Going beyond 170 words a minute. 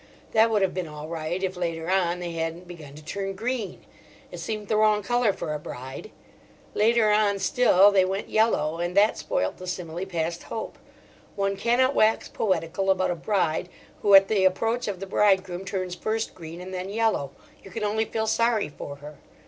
Yes: average, 195 wpm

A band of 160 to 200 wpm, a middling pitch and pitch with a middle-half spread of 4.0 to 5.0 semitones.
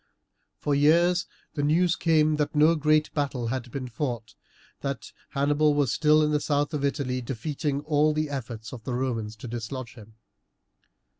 No: average, 165 wpm; medium, 145 Hz; average, 3.3 semitones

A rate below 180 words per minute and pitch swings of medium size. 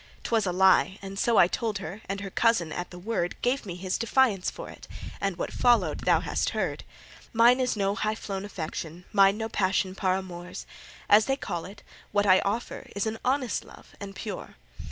No: fast, 205 wpm; average, 3.2 semitones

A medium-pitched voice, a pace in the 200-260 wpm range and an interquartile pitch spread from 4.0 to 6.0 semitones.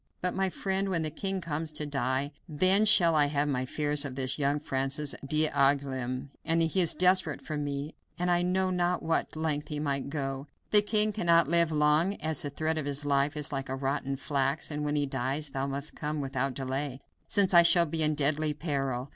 No: medium, 150 Hz; fast, 205 wpm; average, 3.2 semitones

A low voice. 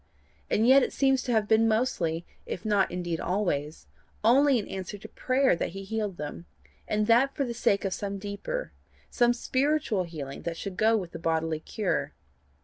No: high, 205 Hz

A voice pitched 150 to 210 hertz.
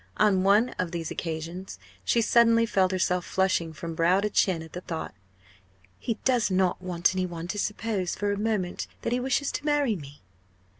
Yes: medium, 185 Hz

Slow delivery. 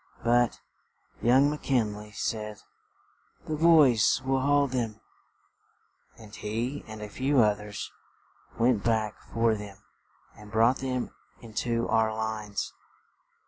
Yes: slow, 125 wpm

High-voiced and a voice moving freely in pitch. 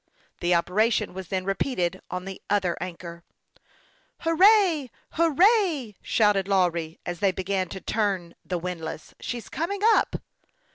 Yes: high, 195 Hz; wide, 7.7 semitones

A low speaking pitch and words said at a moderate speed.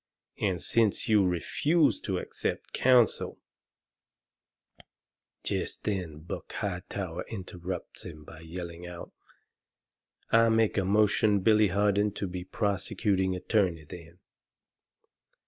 No: very low, 95 Hz; slow, 105 wpm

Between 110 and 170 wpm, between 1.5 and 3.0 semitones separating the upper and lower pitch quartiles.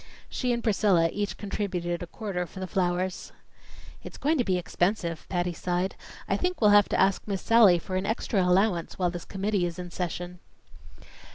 No: average, 185 wpm; average, 2.7 semitones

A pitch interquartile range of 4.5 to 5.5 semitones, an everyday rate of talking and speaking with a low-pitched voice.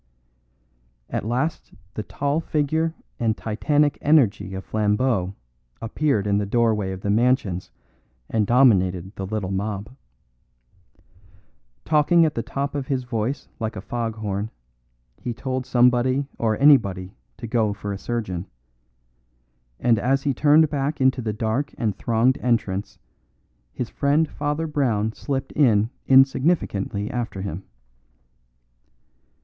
No: average, 4.9 semitones; slow, 130 wpm; low, 115 Hz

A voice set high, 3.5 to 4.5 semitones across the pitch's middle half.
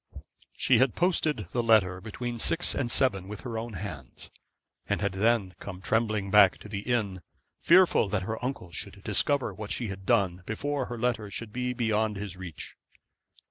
No: low, 110 Hz; average, 3.8 semitones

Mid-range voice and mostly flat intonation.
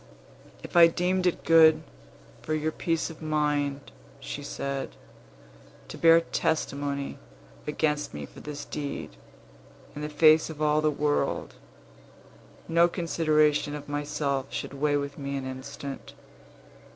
Yes: medium, 150 Hz; narrow, 1.9 semitones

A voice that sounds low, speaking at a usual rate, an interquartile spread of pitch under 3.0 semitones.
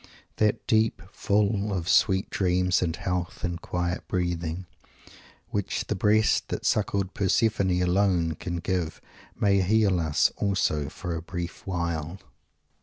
No: very low, 90 Hz; slow, 130 wpm; narrow, 2.4 semitones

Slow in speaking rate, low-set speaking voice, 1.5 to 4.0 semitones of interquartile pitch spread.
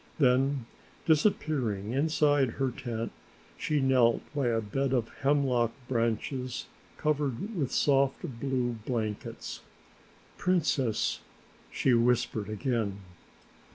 Yes: slow, 95 wpm; low, 130 Hz; average, 3.3 semitones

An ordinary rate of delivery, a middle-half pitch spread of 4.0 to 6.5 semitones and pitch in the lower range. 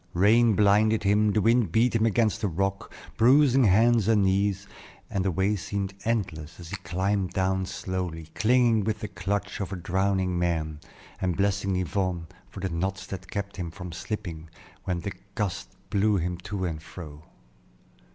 No: average, 170 wpm; average, 2.9 semitones; very low, 95 Hz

